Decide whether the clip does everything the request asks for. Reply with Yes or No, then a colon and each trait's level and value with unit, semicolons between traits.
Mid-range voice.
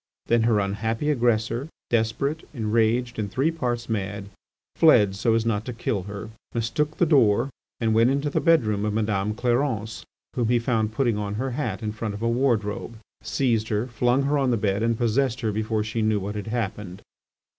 No: low, 115 Hz